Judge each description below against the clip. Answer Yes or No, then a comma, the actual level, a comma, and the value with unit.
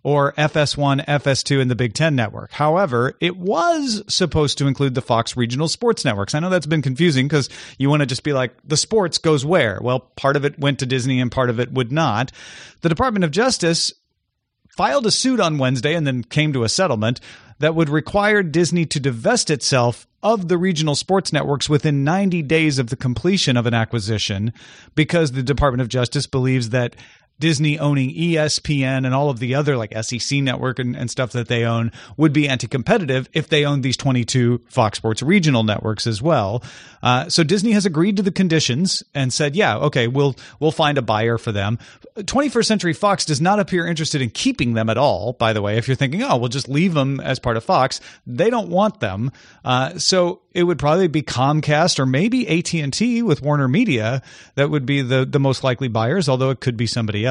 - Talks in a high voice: No, medium, 140 Hz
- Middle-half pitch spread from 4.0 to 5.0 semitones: Yes, average, 4.6 semitones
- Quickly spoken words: Yes, fast, 210 wpm